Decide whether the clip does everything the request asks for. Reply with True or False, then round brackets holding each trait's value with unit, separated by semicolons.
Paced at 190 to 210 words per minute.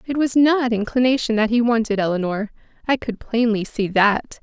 False (175 wpm)